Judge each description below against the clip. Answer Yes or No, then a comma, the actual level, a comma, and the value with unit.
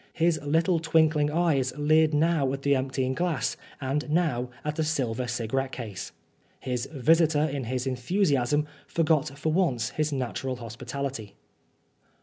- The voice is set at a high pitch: No, medium, 140 Hz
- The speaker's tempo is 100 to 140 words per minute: Yes, slow, 135 wpm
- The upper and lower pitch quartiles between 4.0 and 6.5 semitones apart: No, average, 3.6 semitones